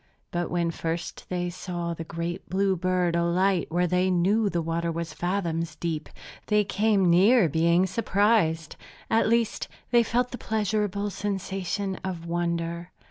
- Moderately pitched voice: Yes, medium, 180 Hz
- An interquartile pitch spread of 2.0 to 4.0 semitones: Yes, average, 3.1 semitones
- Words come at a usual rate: Yes, average, 145 wpm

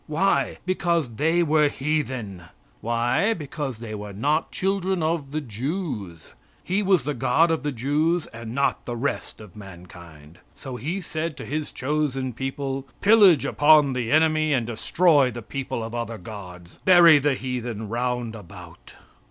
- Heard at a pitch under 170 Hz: Yes, low, 135 Hz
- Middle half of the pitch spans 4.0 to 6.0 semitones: Yes, average, 5.3 semitones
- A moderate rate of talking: Yes, average, 160 wpm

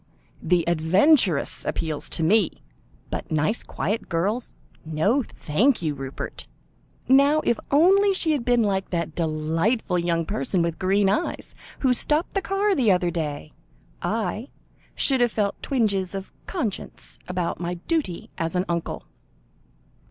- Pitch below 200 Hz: Yes, high, 190 Hz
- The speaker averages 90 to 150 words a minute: Yes, average, 140 wpm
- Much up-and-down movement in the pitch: Yes, wide, 7.0 semitones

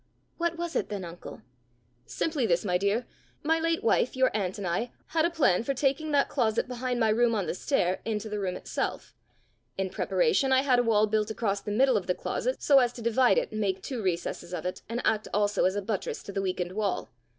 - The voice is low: No, high, 220 Hz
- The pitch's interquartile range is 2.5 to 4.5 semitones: No, average, 5.2 semitones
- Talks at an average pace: No, fast, 230 wpm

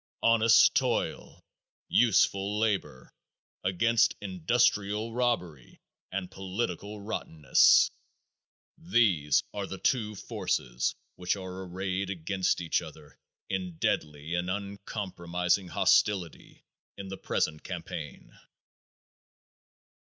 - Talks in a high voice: No, very low, 95 Hz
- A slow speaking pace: Yes, slow, 90 wpm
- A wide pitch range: No, average, 3.0 semitones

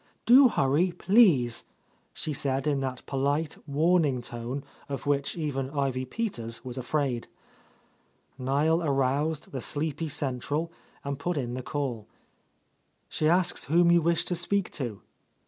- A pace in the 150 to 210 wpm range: No, average, 140 wpm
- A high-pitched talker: No, medium, 145 Hz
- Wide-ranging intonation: No, average, 3.8 semitones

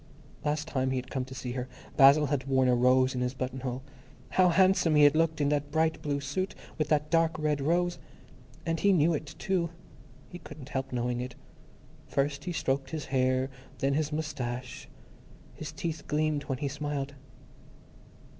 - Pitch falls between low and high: Yes, medium, 145 Hz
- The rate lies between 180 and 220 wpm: Yes, average, 185 wpm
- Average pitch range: Yes, average, 3.2 semitones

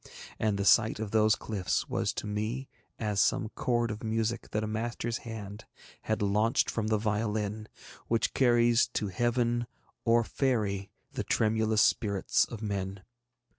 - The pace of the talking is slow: No, average, 155 wpm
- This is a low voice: Yes, low, 110 Hz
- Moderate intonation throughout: No, narrow, 2.0 semitones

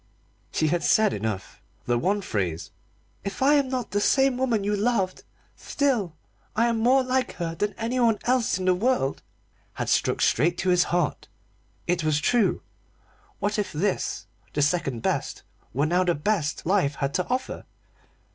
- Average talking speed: Yes, average, 165 wpm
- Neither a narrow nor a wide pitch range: No, wide, 6.9 semitones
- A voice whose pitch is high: Yes, high, 195 Hz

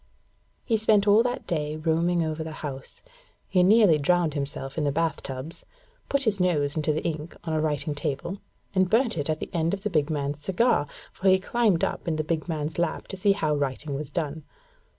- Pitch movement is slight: No, average, 4.0 semitones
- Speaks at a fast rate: Yes, fast, 210 wpm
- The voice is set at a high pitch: No, medium, 160 Hz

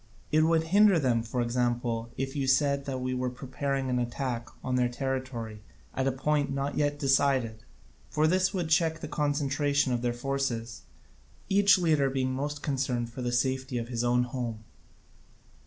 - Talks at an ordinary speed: Yes, average, 170 wpm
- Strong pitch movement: No, average, 2.9 semitones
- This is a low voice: Yes, low, 130 Hz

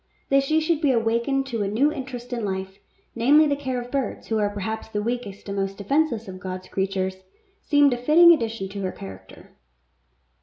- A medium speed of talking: Yes, average, 195 wpm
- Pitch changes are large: Yes, wide, 5.8 semitones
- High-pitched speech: Yes, high, 230 Hz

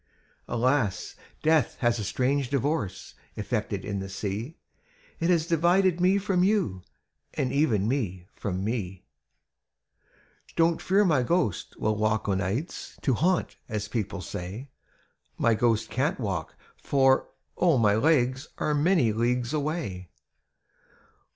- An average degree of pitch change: No, wide, 7.1 semitones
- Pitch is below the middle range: Yes, low, 125 Hz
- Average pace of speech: No, slow, 130 wpm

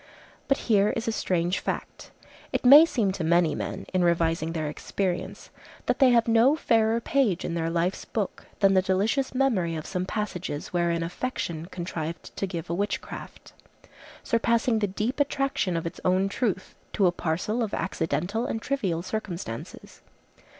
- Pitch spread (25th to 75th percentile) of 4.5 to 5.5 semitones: Yes, average, 5.1 semitones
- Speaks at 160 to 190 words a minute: Yes, average, 165 wpm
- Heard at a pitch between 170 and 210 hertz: Yes, high, 190 Hz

